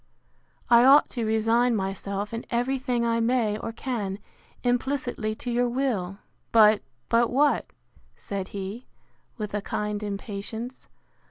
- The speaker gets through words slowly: Yes, slow, 125 wpm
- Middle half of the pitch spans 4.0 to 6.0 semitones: No, average, 3.0 semitones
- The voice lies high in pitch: Yes, high, 230 Hz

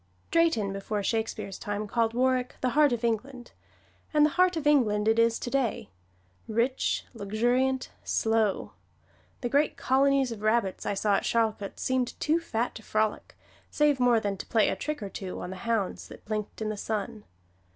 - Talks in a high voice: Yes, high, 230 Hz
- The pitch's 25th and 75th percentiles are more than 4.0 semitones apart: No, average, 3.5 semitones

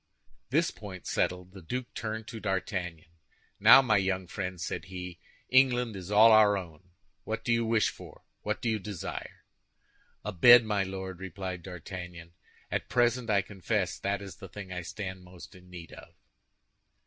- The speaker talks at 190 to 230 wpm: No, average, 170 wpm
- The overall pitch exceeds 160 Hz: No, very low, 95 Hz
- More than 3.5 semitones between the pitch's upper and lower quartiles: No, average, 3.2 semitones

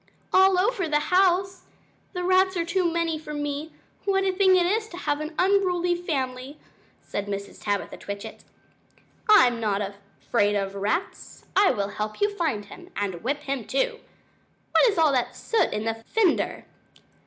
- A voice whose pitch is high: Yes, very high, 325 Hz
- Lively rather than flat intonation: Yes, wide, 8.9 semitones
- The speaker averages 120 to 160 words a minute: No, average, 170 wpm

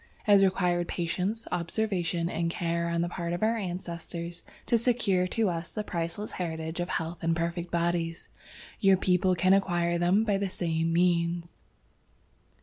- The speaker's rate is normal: Yes, average, 160 wpm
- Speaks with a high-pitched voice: No, medium, 175 Hz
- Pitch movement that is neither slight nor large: No, narrow, 2.1 semitones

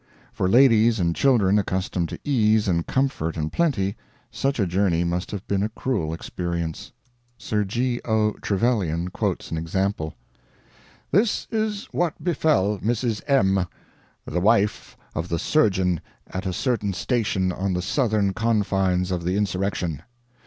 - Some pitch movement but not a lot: Yes, average, 4.5 semitones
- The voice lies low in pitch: Yes, low, 100 Hz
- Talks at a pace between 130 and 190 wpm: Yes, average, 145 wpm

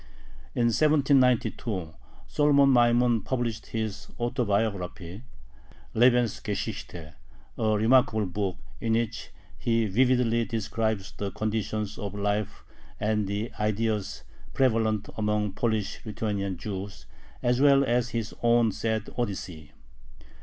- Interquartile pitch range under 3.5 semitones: Yes, narrow, 2.6 semitones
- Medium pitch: No, low, 110 Hz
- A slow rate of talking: Yes, slow, 105 wpm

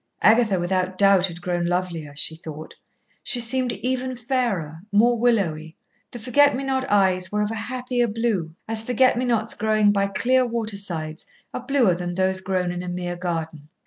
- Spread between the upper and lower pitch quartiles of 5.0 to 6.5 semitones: Yes, average, 5.3 semitones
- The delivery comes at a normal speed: Yes, average, 180 wpm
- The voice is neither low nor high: No, high, 200 Hz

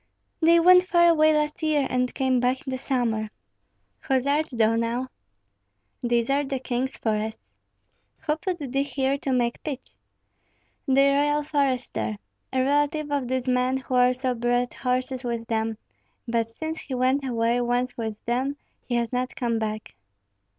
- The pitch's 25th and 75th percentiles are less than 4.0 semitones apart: Yes, average, 2.8 semitones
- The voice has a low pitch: No, very high, 255 Hz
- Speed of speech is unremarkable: Yes, average, 160 wpm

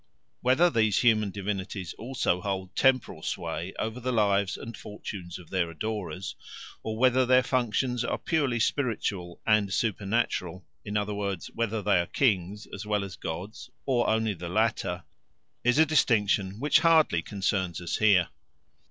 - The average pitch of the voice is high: No, low, 105 Hz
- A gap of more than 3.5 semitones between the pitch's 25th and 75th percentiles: Yes, average, 4.1 semitones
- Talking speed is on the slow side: No, average, 150 wpm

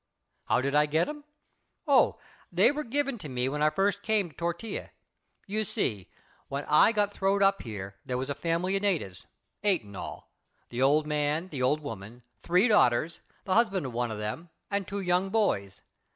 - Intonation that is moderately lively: No, wide, 7.6 semitones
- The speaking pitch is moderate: Yes, medium, 165 Hz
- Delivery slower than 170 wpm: No, average, 195 wpm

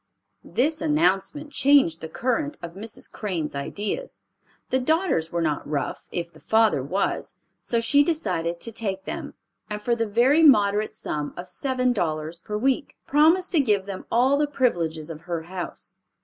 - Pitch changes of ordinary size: No, wide, 8.2 semitones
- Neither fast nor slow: Yes, average, 165 wpm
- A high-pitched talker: Yes, high, 210 Hz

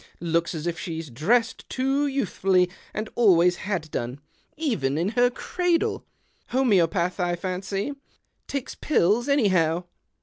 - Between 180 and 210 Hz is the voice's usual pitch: Yes, medium, 185 Hz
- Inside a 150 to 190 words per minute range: No, slow, 135 wpm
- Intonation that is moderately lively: No, wide, 6.5 semitones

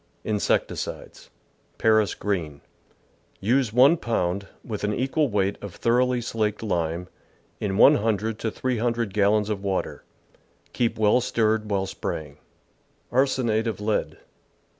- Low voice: Yes, low, 110 Hz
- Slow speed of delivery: Yes, slow, 120 wpm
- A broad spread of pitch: No, average, 2.8 semitones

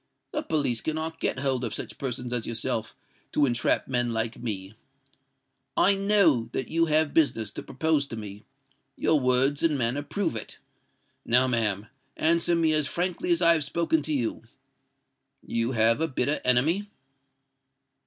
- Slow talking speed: No, average, 160 wpm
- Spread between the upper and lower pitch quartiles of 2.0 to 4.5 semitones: No, wide, 5.5 semitones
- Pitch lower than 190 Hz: Yes, medium, 140 Hz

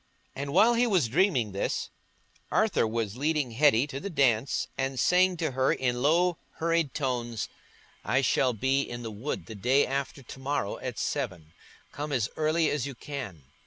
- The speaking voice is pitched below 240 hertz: Yes, low, 135 Hz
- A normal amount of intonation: Yes, average, 4.2 semitones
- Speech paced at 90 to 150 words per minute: No, average, 175 wpm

